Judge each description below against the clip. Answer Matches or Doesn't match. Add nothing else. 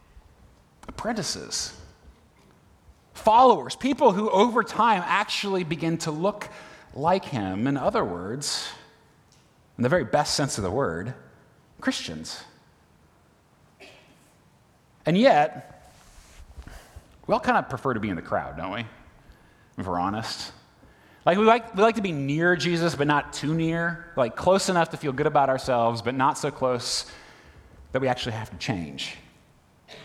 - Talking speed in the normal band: Matches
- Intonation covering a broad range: Matches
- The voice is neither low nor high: Matches